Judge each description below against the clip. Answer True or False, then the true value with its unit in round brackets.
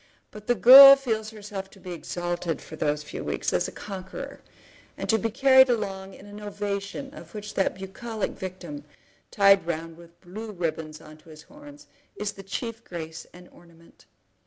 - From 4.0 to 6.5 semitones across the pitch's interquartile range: True (4.4 semitones)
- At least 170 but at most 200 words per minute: True (180 wpm)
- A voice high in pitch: True (195 Hz)